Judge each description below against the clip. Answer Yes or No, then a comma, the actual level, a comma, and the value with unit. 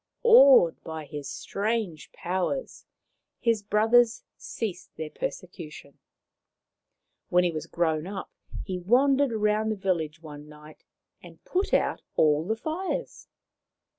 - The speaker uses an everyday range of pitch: No, wide, 6.8 semitones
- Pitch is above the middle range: Yes, high, 195 Hz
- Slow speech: Yes, slow, 120 wpm